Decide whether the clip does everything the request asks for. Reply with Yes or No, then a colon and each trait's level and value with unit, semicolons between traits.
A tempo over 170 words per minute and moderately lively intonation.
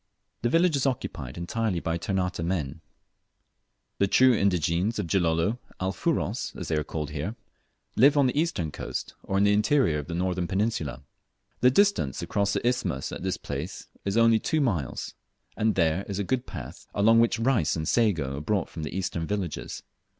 No: average, 180 wpm; wide, 5.7 semitones